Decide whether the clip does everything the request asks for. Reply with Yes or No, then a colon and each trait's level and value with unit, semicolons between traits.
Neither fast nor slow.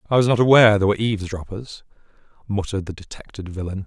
Yes: average, 170 wpm